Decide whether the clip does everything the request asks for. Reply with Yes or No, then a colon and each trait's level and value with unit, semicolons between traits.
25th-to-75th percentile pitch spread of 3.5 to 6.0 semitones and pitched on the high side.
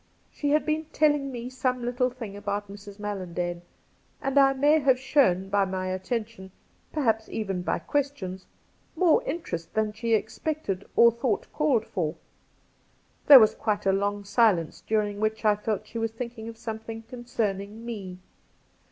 Yes: average, 4.2 semitones; high, 220 Hz